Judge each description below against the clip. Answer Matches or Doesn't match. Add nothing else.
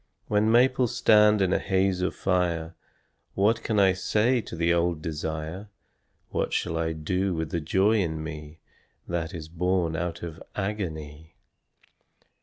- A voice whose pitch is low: Matches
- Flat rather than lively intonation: Doesn't match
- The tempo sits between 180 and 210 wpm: Doesn't match